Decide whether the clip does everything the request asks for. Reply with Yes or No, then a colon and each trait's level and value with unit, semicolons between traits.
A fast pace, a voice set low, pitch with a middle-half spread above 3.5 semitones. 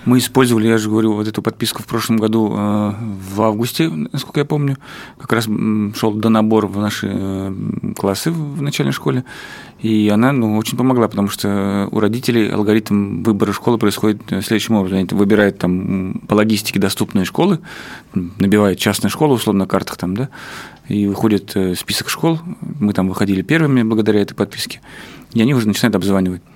No: fast, 165 wpm; low, 110 Hz; average, 2.7 semitones